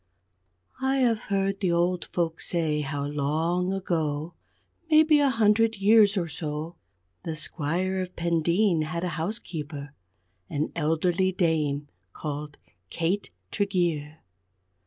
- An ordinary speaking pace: No, slow, 115 wpm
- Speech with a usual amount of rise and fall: Yes, average, 4.0 semitones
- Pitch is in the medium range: Yes, medium, 170 Hz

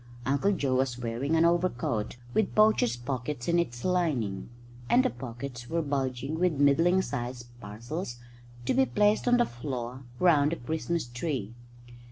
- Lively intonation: Yes, wide, 6.1 semitones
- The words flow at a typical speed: Yes, average, 155 wpm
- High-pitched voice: No, medium, 140 Hz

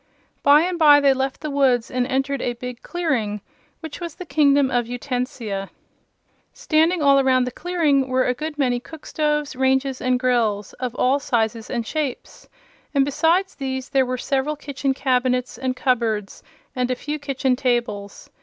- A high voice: Yes, very high, 265 Hz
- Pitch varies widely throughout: No, narrow, 2.6 semitones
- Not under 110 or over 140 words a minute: No, average, 170 wpm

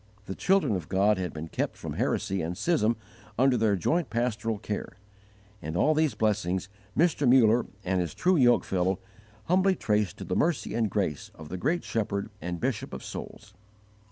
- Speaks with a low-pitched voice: Yes, low, 105 Hz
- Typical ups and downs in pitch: No, wide, 5.7 semitones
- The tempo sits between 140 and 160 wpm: No, average, 180 wpm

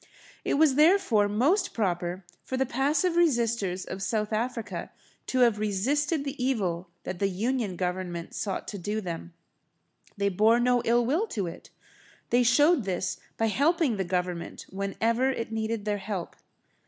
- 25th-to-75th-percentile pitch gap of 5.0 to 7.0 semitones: Yes, average, 5.3 semitones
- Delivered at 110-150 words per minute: No, average, 160 wpm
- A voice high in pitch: Yes, high, 220 Hz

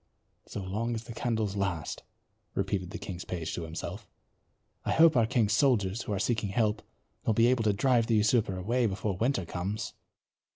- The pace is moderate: Yes, average, 180 wpm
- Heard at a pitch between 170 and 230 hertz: No, low, 105 Hz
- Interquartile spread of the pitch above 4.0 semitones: No, average, 3.5 semitones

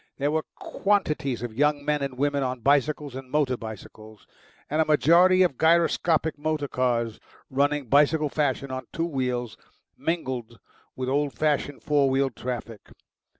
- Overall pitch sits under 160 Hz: Yes, medium, 140 Hz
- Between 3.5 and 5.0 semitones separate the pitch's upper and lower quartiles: No, average, 3.1 semitones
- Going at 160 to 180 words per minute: No, average, 150 wpm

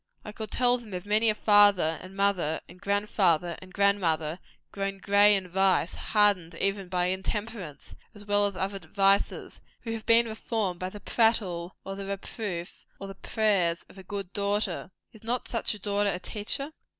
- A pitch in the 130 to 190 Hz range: No, high, 200 Hz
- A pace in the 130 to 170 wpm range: No, average, 185 wpm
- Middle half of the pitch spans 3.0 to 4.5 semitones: No, narrow, 2.4 semitones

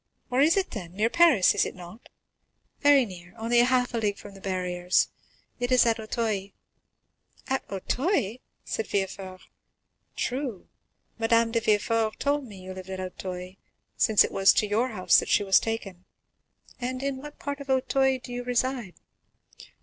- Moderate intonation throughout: Yes, average, 5.0 semitones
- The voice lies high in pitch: Yes, high, 225 Hz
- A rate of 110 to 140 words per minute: No, average, 165 wpm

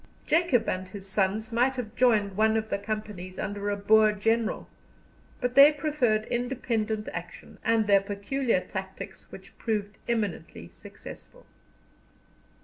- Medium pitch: No, high, 215 Hz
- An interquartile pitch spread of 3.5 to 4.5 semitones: No, average, 3.1 semitones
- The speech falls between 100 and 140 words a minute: Yes, slow, 135 wpm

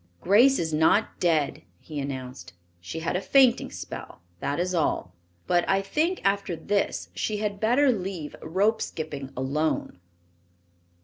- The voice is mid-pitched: Yes, medium, 175 Hz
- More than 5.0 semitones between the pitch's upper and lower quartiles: Yes, wide, 5.5 semitones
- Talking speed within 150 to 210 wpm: No, average, 140 wpm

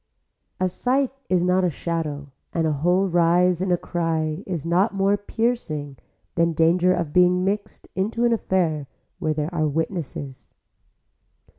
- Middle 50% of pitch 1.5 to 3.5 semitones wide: Yes, average, 3.0 semitones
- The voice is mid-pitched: Yes, medium, 175 Hz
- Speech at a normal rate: Yes, average, 150 wpm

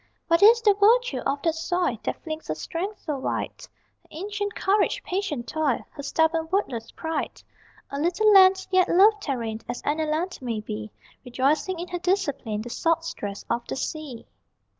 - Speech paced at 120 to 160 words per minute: No, average, 175 wpm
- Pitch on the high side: Yes, very high, 325 Hz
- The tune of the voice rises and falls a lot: Yes, wide, 5.8 semitones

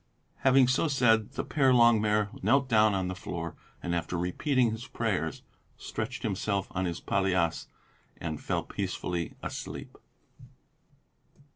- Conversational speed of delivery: No, slow, 130 wpm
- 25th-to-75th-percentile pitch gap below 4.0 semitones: No, wide, 5.6 semitones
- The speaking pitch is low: Yes, low, 105 Hz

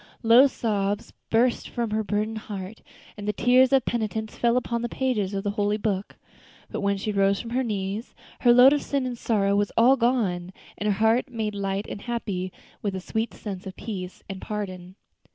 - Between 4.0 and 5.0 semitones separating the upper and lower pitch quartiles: No, average, 3.1 semitones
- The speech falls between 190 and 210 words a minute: Yes, average, 200 wpm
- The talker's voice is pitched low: No, high, 215 Hz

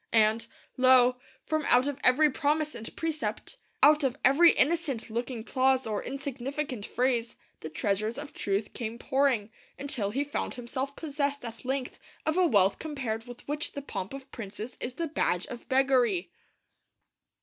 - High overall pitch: Yes, very high, 260 Hz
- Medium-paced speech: Yes, average, 160 wpm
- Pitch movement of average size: Yes, average, 3.8 semitones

